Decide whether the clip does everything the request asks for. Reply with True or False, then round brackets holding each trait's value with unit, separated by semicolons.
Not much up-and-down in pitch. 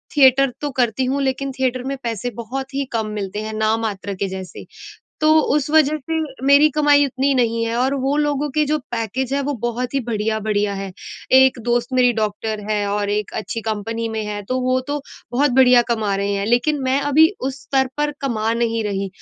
False (4.0 semitones)